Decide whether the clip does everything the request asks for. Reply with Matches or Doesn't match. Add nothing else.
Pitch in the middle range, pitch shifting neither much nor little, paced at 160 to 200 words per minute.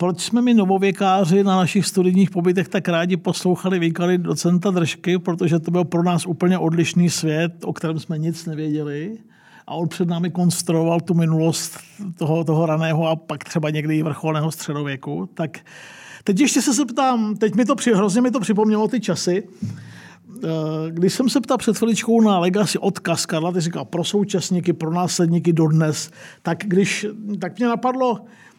Matches